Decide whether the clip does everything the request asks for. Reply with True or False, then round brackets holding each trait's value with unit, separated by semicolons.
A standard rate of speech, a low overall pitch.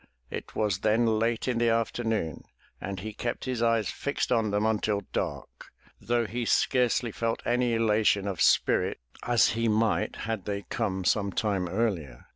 True (165 wpm; 110 Hz)